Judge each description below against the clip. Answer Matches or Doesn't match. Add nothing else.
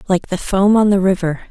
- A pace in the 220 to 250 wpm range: Matches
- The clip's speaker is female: Matches